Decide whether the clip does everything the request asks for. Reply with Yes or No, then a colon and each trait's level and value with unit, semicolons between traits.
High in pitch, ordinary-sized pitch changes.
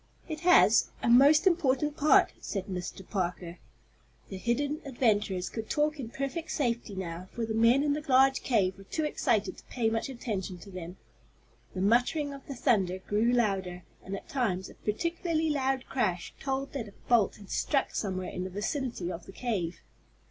No: high, 235 Hz; wide, 6.4 semitones